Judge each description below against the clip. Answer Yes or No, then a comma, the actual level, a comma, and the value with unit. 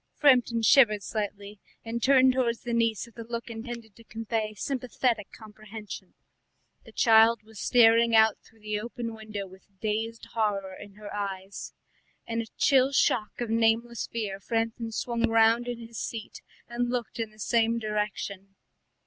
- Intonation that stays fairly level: Yes, narrow, 1.8 semitones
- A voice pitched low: No, high, 225 Hz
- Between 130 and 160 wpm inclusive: Yes, average, 155 wpm